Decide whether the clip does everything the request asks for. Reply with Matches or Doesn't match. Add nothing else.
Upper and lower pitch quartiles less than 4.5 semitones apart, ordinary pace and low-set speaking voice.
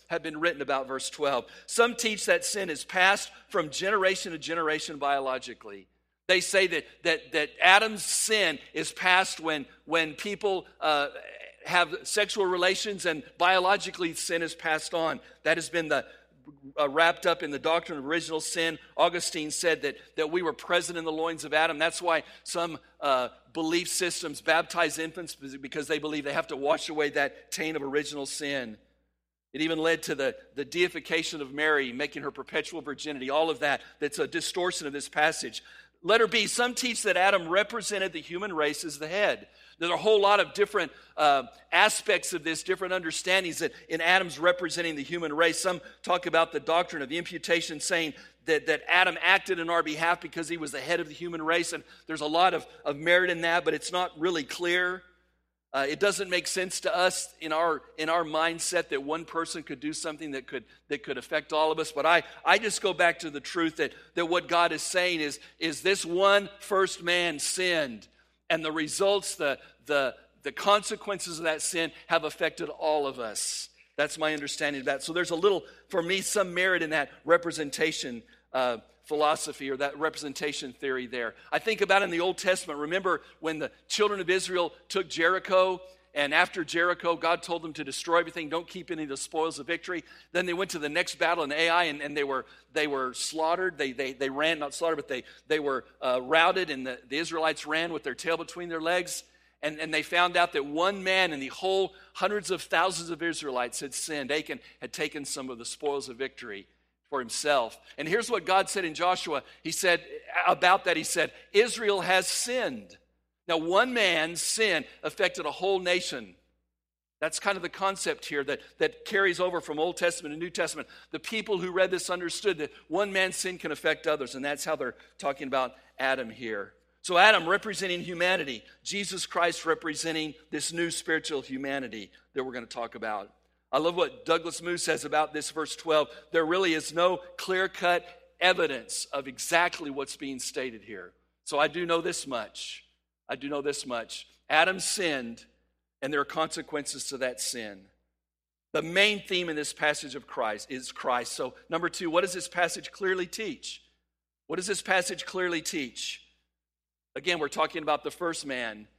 Doesn't match